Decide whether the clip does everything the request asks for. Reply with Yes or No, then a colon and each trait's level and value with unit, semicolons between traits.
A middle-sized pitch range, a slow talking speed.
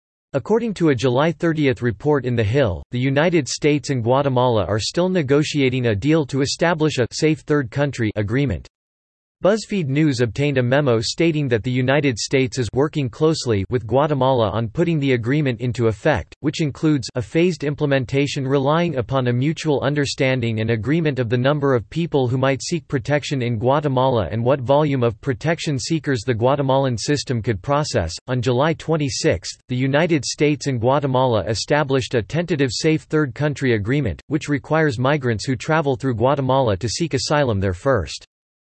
No: average, 3.2 semitones; average, 170 wpm